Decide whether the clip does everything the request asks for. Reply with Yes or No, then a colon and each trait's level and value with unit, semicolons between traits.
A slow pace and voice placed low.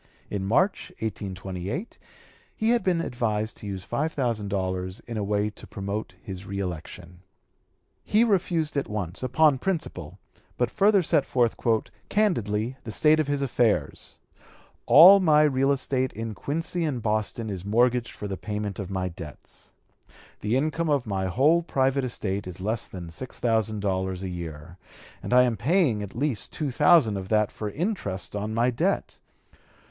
No: average, 160 wpm; low, 115 Hz